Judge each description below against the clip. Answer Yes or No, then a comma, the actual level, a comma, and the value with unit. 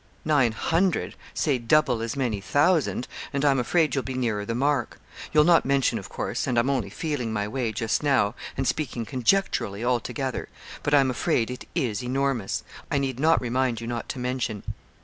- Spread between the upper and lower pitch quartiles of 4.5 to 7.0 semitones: No, average, 3.5 semitones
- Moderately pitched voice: No, low, 130 Hz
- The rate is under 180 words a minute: No, average, 185 wpm